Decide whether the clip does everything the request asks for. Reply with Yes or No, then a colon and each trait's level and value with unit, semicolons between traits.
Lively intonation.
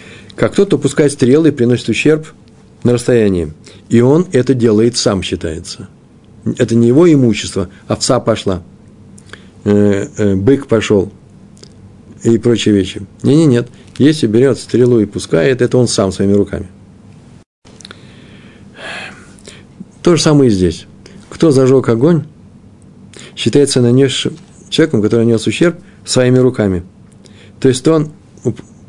No: average, 4.7 semitones